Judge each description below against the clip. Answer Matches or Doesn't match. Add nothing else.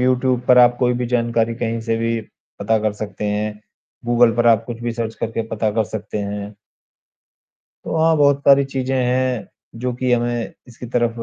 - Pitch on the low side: Matches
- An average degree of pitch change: Doesn't match